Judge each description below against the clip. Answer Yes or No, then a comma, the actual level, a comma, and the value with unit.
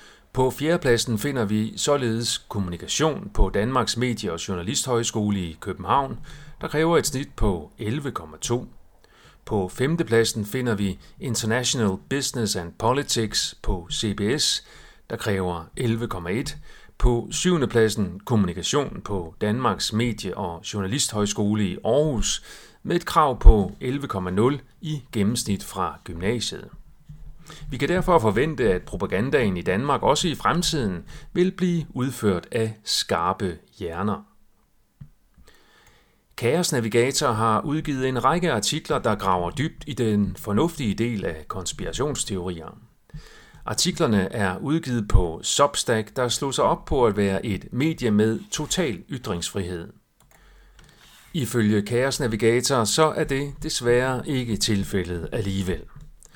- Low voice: Yes, low, 115 Hz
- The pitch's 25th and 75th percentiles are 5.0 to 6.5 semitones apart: Yes, wide, 5.5 semitones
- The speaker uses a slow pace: Yes, slow, 120 wpm